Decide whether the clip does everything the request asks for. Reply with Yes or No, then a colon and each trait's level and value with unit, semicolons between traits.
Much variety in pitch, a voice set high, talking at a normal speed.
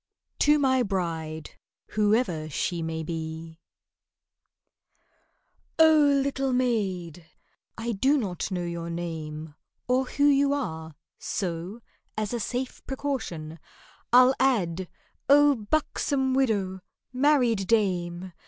No: wide, 7.7 semitones; high, 210 Hz; slow, 95 wpm